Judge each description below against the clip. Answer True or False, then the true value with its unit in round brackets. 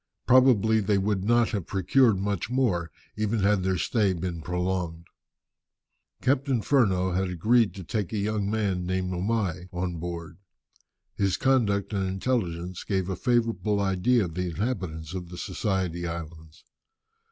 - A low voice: True (95 Hz)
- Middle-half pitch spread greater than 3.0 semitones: True (3.6 semitones)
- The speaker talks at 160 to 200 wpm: False (145 wpm)